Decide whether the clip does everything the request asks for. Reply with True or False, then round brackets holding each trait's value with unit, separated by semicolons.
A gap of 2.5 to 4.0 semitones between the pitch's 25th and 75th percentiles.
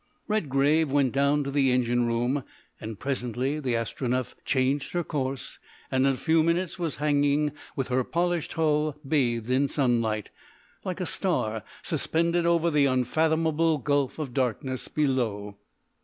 True (3.4 semitones)